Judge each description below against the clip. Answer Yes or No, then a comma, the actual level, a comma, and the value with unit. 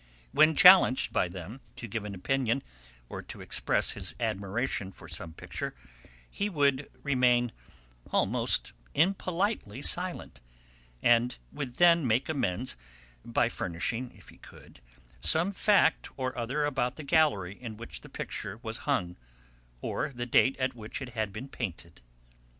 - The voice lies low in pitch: Yes, low, 125 Hz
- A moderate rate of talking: Yes, average, 145 wpm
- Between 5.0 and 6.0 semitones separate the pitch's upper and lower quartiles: Yes, wide, 5.4 semitones